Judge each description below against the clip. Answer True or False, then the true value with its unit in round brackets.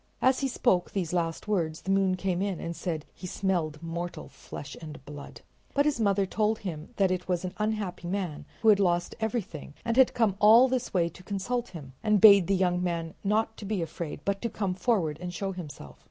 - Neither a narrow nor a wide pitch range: True (3.8 semitones)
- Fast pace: True (215 wpm)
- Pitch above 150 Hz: True (185 Hz)